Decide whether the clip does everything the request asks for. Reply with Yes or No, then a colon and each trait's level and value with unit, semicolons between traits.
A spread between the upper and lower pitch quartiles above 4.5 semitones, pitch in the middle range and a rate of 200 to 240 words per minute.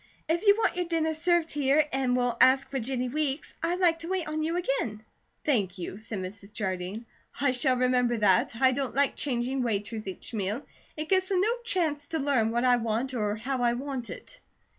No: average, 5.2 semitones; very high, 260 Hz; fast, 205 wpm